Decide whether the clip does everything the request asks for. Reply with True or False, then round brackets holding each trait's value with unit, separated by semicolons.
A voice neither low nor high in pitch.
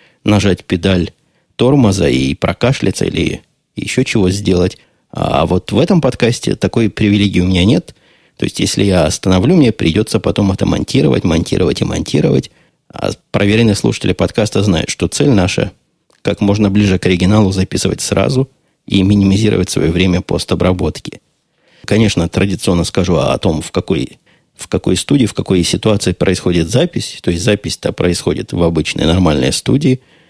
False (95 Hz)